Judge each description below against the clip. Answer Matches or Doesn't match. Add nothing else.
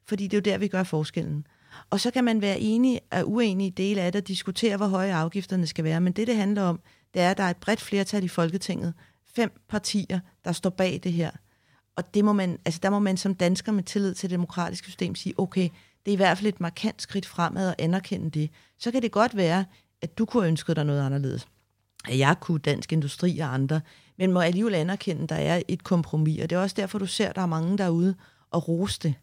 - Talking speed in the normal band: Doesn't match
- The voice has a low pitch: Doesn't match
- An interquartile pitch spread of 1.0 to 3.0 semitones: Doesn't match